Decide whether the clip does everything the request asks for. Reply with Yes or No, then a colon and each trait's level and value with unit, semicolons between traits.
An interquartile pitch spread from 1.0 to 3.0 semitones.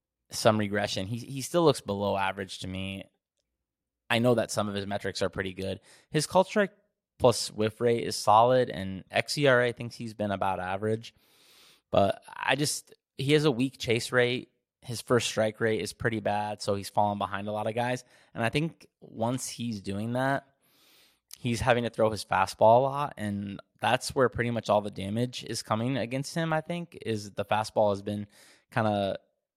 No: average, 3.6 semitones